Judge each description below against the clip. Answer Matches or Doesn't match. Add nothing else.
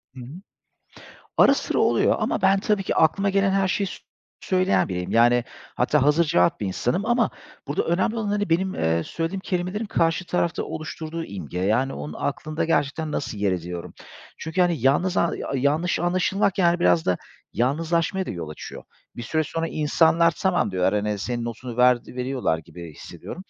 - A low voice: Doesn't match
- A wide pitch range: Matches